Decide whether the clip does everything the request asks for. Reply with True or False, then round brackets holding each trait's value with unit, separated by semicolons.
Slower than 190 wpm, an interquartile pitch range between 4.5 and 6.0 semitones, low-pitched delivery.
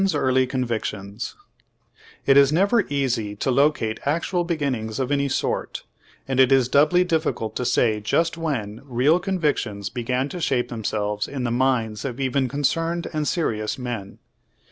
True (155 wpm; 4.8 semitones; 130 Hz)